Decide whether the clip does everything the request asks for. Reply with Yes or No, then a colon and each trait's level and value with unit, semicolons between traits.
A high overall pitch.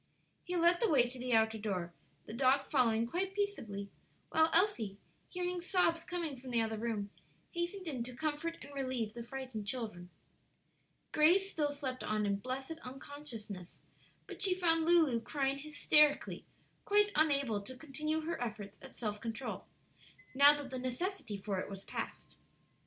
Yes: very high, 270 Hz